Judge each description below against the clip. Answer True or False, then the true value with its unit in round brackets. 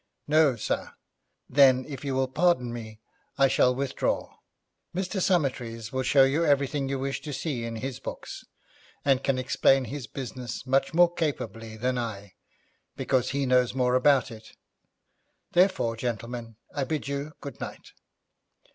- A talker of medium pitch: False (130 Hz)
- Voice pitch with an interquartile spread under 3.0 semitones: True (2.6 semitones)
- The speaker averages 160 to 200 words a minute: False (150 wpm)